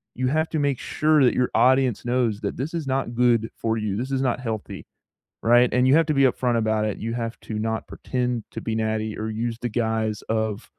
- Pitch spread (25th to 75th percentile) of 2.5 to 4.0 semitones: Yes, average, 2.8 semitones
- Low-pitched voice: Yes, low, 120 Hz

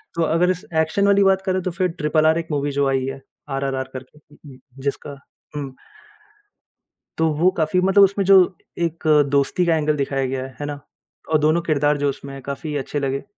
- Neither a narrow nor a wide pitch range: Yes, average, 3.7 semitones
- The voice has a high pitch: No, medium, 150 Hz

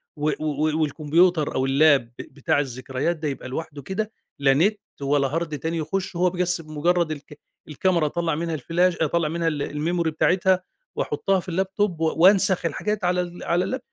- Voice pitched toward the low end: No, medium, 165 Hz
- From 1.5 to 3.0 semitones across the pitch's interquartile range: No, average, 3.4 semitones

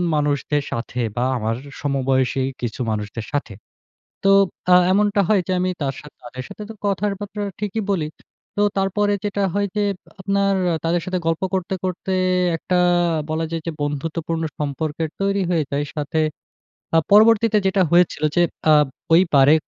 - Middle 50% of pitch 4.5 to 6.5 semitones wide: Yes, wide, 5.5 semitones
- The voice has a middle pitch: Yes, medium, 165 Hz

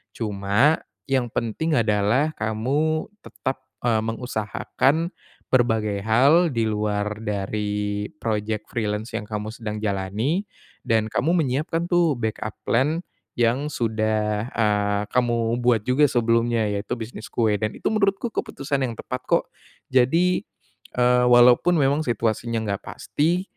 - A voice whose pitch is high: No, low, 115 Hz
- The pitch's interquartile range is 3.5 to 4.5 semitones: Yes, average, 4.0 semitones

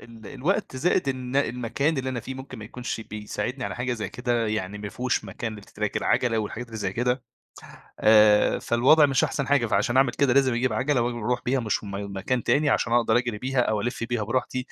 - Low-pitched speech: Yes, low, 120 Hz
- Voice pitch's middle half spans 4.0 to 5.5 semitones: No, average, 3.1 semitones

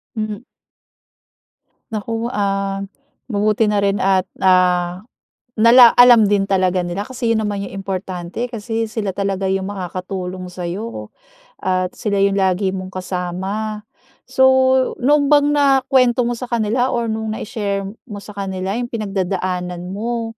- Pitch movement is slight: No, average, 3.3 semitones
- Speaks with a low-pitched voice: No, high, 200 Hz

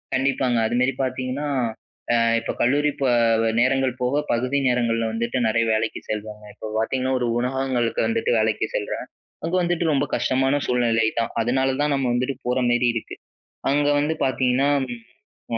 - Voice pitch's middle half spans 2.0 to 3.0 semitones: Yes, narrow, 2.5 semitones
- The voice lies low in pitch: Yes, low, 125 Hz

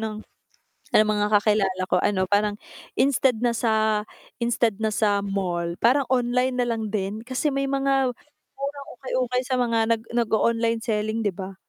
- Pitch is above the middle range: Yes, high, 225 Hz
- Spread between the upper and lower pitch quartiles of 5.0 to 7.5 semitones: No, average, 3.2 semitones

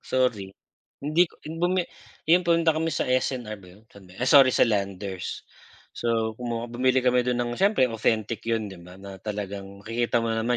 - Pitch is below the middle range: Yes, low, 115 Hz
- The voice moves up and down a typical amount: Yes, average, 4.1 semitones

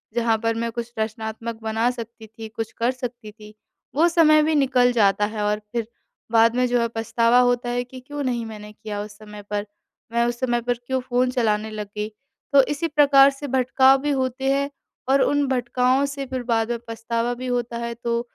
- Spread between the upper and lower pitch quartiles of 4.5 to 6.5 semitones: No, average, 2.8 semitones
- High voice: Yes, high, 240 Hz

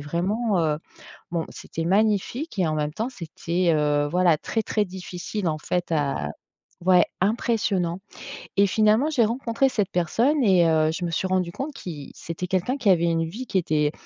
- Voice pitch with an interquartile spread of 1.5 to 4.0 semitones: No, average, 4.7 semitones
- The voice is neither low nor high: Yes, medium, 180 Hz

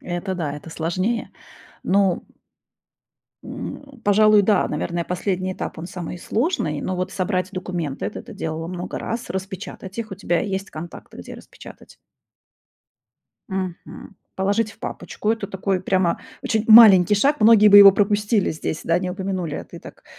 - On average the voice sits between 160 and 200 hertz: Yes, high, 190 Hz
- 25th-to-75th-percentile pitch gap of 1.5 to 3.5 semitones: Yes, average, 2.9 semitones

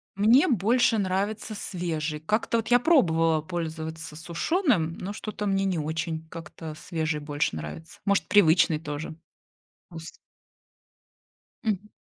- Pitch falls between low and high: Yes, medium, 170 Hz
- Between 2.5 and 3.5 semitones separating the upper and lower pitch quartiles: No, average, 4.7 semitones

